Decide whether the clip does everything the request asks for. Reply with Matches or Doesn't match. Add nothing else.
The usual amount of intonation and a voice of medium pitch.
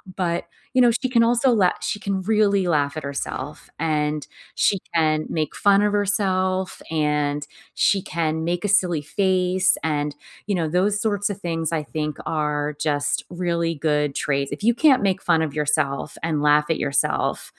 Matches